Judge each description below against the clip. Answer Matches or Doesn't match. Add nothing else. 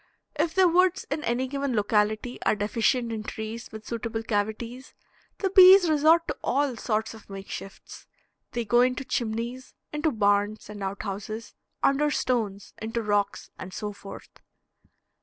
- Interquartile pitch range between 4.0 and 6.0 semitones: Matches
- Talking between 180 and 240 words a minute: Doesn't match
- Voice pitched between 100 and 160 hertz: Doesn't match